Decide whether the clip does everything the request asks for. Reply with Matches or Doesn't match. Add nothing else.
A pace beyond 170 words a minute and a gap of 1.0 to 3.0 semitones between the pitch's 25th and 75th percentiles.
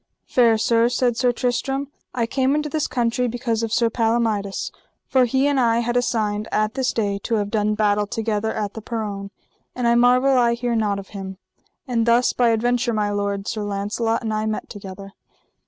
Matches